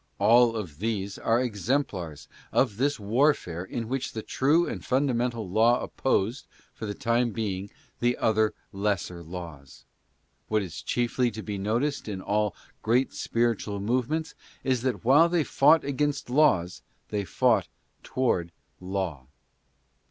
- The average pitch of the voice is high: No, low, 115 Hz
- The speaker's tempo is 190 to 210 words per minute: No, slow, 135 wpm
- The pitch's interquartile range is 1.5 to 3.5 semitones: No, average, 4.7 semitones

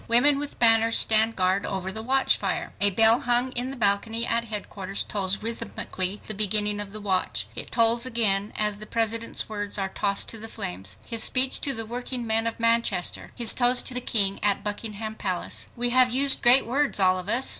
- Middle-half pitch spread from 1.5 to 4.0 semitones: Yes, average, 3.0 semitones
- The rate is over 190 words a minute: Yes, average, 200 wpm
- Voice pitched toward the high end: Yes, high, 225 Hz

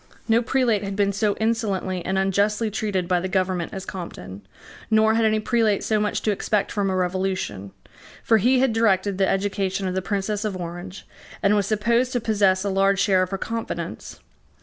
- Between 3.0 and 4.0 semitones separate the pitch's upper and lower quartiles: No, narrow, 2.5 semitones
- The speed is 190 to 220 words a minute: Yes, average, 195 wpm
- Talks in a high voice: Yes, high, 200 Hz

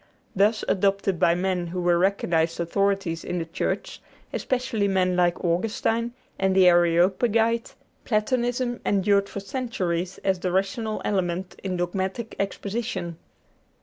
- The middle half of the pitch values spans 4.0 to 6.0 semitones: No, average, 3.3 semitones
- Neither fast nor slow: No, slow, 125 wpm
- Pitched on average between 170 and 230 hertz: Yes, high, 190 Hz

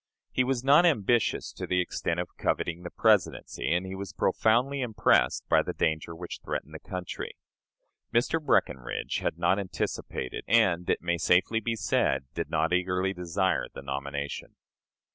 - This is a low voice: Yes, very low, 90 Hz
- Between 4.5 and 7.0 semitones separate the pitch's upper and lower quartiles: Yes, average, 5.0 semitones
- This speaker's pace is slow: No, average, 160 wpm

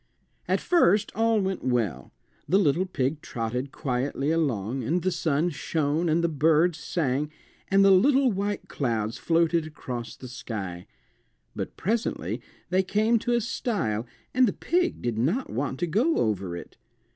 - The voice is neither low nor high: Yes, medium, 160 Hz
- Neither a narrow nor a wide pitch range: No, wide, 7.8 semitones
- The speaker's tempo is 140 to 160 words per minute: Yes, average, 155 wpm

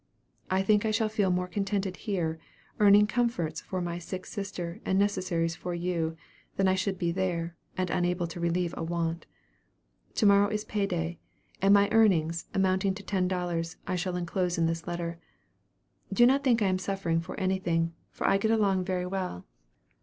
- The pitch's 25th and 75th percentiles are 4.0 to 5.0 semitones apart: No, average, 2.7 semitones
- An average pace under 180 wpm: No, average, 185 wpm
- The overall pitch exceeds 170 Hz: Yes, medium, 185 Hz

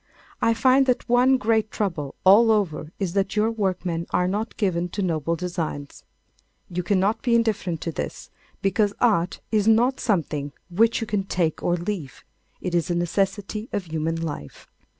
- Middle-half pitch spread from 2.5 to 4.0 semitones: No, average, 4.5 semitones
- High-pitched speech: Yes, high, 195 Hz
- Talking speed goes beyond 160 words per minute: Yes, average, 170 wpm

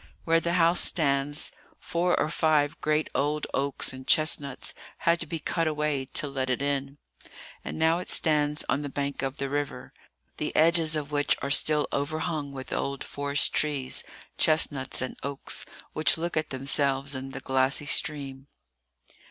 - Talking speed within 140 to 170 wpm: Yes, average, 165 wpm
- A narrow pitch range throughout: Yes, narrow, 2.2 semitones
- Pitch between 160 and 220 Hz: No, medium, 145 Hz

